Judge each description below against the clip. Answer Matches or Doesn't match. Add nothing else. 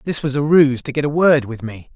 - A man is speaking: Matches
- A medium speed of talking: Doesn't match